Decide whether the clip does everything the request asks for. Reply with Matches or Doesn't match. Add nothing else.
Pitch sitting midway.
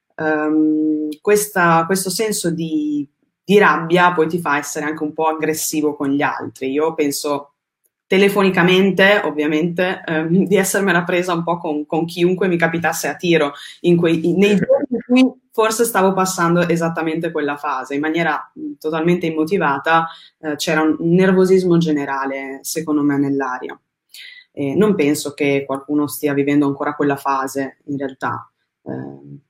Matches